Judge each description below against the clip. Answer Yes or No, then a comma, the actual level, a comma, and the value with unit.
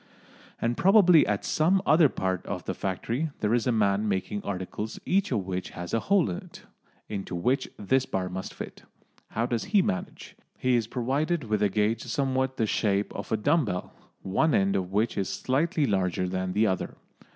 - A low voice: Yes, low, 110 Hz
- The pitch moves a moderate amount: No, wide, 5.7 semitones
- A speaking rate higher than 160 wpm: Yes, average, 195 wpm